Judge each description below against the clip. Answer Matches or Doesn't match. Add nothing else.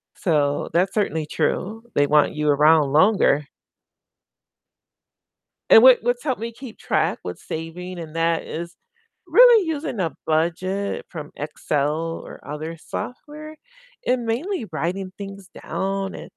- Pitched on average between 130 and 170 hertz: Doesn't match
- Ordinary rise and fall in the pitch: Doesn't match